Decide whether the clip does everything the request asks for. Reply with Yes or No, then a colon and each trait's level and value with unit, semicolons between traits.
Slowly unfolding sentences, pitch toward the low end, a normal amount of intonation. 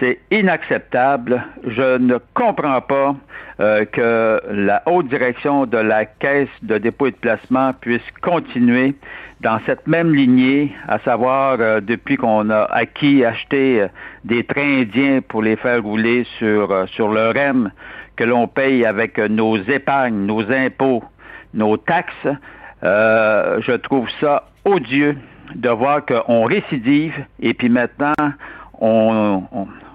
Yes: slow, 140 wpm; low, 125 Hz; average, 3.7 semitones